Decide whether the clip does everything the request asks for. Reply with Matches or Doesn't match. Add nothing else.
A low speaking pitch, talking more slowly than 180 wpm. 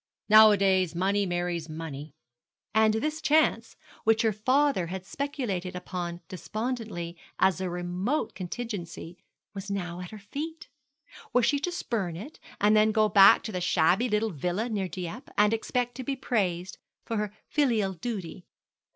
Doesn't match